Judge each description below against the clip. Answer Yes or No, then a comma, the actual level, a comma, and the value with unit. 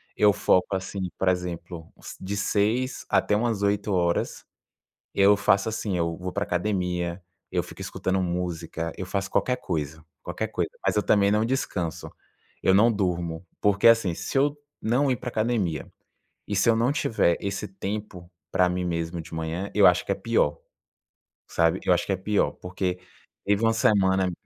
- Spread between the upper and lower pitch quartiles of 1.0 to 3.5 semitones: Yes, average, 3.1 semitones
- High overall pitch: No, very low, 95 Hz